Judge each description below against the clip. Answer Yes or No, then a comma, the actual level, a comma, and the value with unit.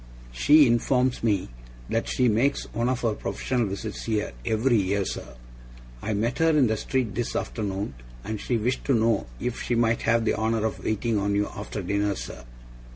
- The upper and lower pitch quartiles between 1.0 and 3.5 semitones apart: Yes, average, 2.8 semitones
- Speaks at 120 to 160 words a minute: No, average, 190 wpm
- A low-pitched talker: Yes, low, 110 Hz